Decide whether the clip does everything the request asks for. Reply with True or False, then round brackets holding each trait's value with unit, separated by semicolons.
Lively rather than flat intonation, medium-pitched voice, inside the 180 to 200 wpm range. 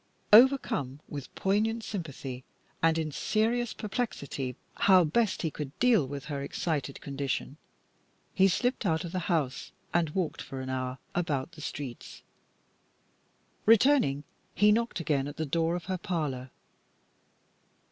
False (6.5 semitones; 165 Hz; 135 wpm)